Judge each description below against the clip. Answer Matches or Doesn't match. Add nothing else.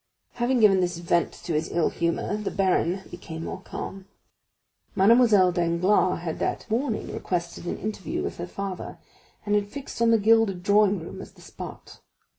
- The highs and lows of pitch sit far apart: Doesn't match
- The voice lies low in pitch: Doesn't match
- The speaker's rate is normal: Matches